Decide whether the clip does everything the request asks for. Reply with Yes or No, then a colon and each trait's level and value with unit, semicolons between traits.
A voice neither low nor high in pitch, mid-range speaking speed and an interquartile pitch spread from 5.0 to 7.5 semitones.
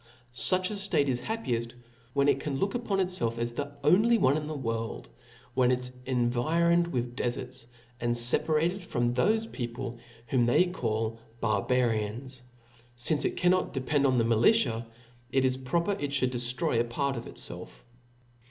No: low, 130 Hz; average, 165 wpm; wide, 5.6 semitones